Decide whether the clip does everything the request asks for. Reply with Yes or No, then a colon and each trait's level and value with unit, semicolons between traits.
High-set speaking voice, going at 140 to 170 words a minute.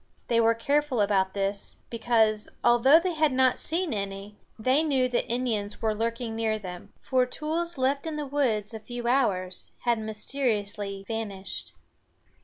Yes: high, 230 Hz; average, 155 wpm